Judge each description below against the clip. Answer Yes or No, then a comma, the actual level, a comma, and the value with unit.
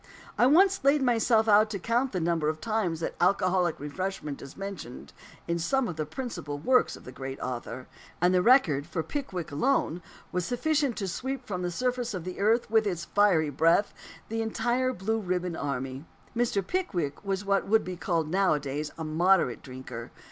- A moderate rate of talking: Yes, average, 185 wpm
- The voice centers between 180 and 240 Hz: Yes, medium, 185 Hz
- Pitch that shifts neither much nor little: No, wide, 6.3 semitones